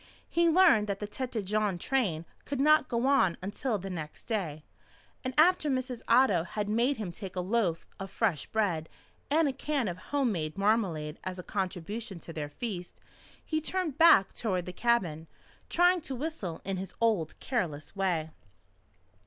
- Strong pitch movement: Yes, wide, 6.4 semitones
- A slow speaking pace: No, average, 170 wpm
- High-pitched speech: Yes, high, 210 Hz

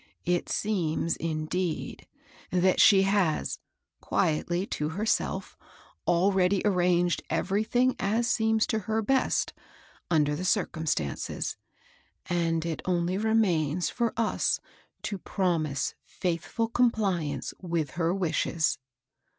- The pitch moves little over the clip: No, average, 4.1 semitones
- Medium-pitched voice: Yes, medium, 180 Hz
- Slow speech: Yes, slow, 100 wpm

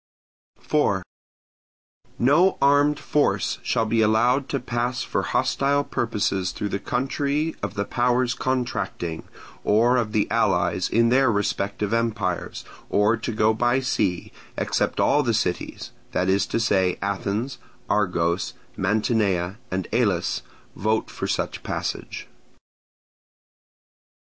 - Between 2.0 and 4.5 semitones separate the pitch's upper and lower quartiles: Yes, average, 4.1 semitones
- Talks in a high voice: No, low, 110 Hz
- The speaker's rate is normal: No, slow, 115 wpm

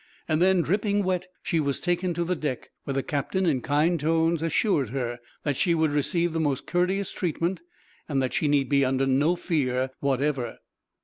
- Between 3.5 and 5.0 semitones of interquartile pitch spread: Yes, average, 4.2 semitones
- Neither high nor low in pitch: Yes, medium, 155 Hz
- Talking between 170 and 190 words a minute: Yes, average, 185 wpm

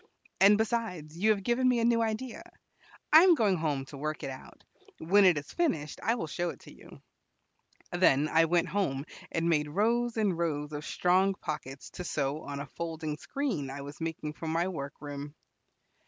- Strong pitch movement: Yes, wide, 5.9 semitones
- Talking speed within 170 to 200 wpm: Yes, average, 195 wpm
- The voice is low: No, medium, 165 Hz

